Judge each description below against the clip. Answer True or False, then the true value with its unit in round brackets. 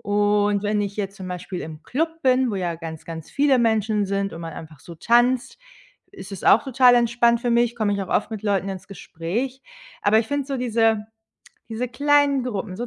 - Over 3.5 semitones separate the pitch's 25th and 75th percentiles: True (4.0 semitones)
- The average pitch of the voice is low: False (215 Hz)